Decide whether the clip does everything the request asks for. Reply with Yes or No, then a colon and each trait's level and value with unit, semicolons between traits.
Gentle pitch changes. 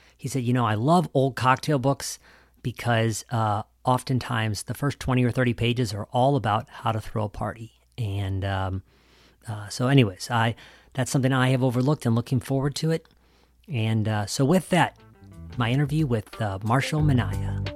No: average, 3.9 semitones